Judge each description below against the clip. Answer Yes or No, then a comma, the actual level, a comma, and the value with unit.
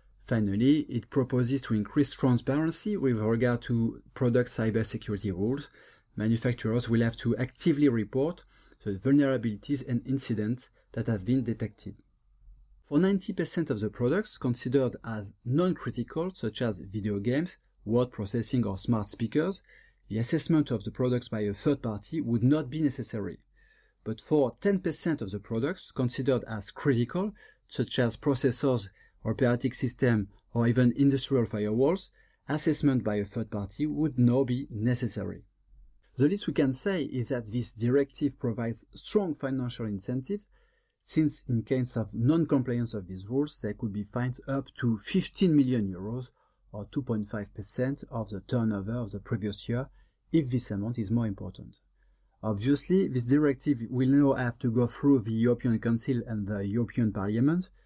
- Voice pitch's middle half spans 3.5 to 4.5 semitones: Yes, average, 3.9 semitones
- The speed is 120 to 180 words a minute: Yes, average, 150 wpm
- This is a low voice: Yes, low, 125 Hz